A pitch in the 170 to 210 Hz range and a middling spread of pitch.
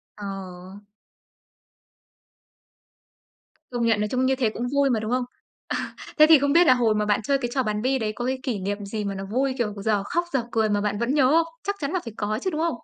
No: high, 235 Hz; average, 4.4 semitones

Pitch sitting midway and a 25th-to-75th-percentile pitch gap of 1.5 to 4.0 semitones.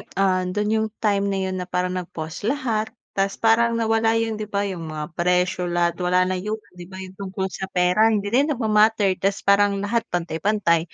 No: high, 195 Hz; average, 3.0 semitones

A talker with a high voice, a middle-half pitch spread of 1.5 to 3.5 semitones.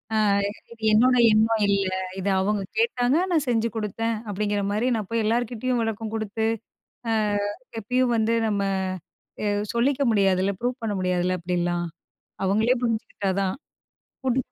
Yes: high, 220 Hz; average, 3.1 semitones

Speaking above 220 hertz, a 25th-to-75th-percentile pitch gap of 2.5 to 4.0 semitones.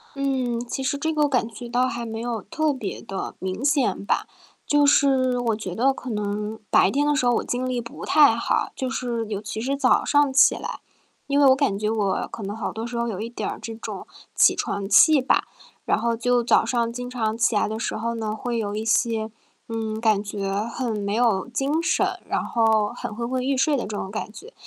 Yes: high, 235 Hz; average, 3.1 semitones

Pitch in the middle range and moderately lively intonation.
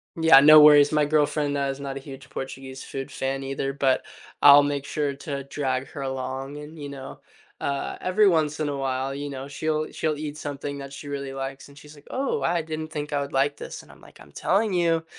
No: medium, 145 Hz; narrow, 1.9 semitones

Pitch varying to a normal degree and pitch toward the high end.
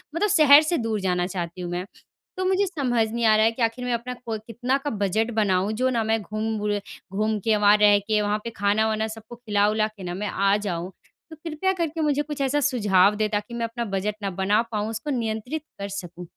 Yes: average, 3.3 semitones; high, 220 Hz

